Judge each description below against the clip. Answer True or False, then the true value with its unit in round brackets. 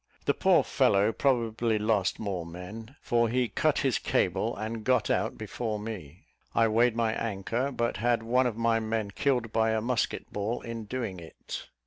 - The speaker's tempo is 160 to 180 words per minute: True (175 wpm)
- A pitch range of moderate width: False (1.9 semitones)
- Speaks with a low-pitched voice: True (115 Hz)